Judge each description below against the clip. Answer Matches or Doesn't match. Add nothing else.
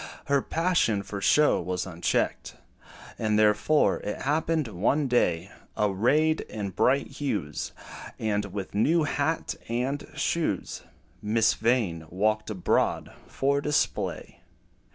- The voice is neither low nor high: Doesn't match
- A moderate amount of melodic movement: Doesn't match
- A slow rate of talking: Matches